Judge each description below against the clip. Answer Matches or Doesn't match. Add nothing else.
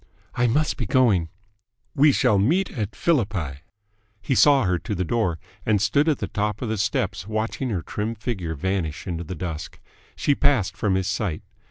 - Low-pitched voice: Matches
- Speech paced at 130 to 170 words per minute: Doesn't match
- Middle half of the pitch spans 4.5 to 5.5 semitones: Matches